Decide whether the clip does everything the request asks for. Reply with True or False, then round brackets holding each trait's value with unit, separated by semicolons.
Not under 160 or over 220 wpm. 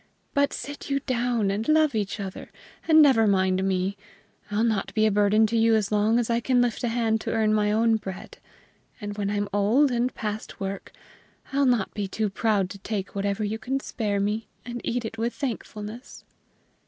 True (200 wpm)